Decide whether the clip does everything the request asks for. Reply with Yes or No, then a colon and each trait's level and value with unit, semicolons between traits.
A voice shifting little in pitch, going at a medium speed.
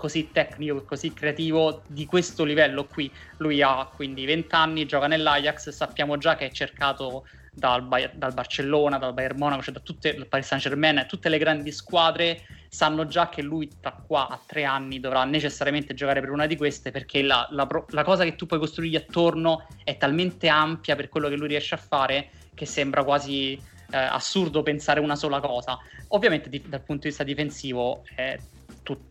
No: narrow, 2.3 semitones; fast, 185 wpm